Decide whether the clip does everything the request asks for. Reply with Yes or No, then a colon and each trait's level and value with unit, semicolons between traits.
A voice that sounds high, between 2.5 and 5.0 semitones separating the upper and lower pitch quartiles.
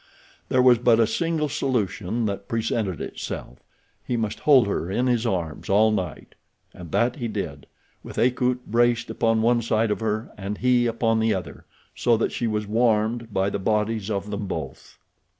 No: low, 110 Hz; average, 3.0 semitones